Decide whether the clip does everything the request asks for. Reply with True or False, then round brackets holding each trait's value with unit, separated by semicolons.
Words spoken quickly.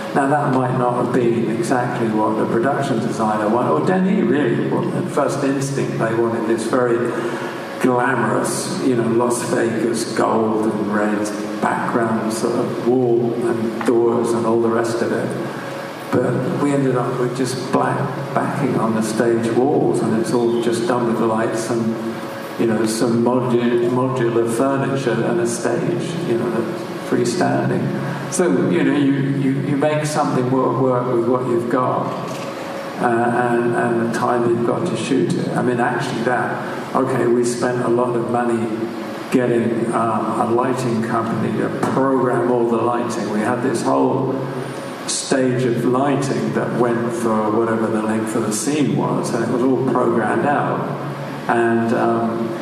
False (165 wpm)